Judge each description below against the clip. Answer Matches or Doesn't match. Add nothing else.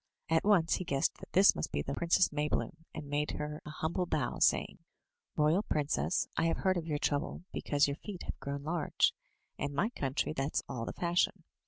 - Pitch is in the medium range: Matches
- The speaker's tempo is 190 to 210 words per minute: Matches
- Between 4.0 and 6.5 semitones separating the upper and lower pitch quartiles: Doesn't match